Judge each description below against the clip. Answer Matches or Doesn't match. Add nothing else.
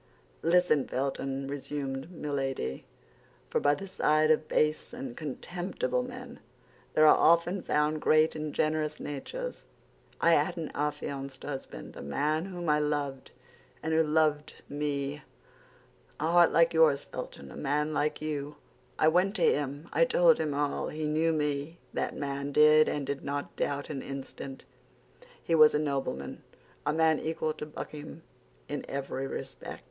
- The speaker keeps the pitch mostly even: Matches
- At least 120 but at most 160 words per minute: Matches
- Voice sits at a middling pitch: Matches